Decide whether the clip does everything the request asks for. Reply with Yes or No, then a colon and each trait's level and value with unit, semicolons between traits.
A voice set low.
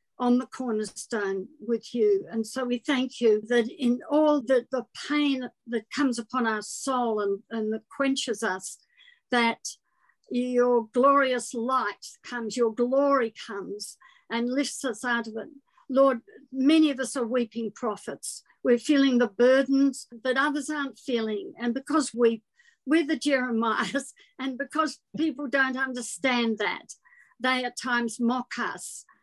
No: very high, 250 Hz